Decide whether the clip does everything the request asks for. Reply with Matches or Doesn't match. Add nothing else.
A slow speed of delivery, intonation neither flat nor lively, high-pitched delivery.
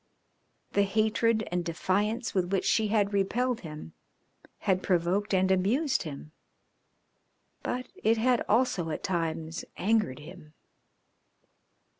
Matches